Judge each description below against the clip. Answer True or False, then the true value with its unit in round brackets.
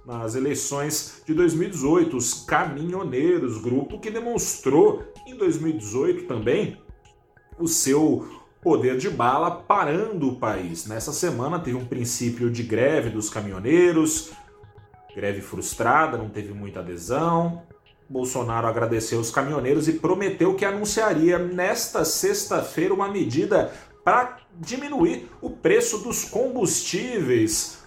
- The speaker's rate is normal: False (115 wpm)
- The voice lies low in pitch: False (150 Hz)